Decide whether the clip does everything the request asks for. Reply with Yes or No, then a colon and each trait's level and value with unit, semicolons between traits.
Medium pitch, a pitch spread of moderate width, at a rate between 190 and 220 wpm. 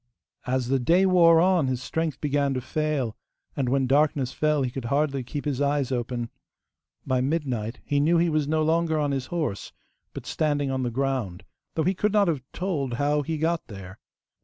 Yes: medium, 145 Hz; average, 3.6 semitones; average, 195 wpm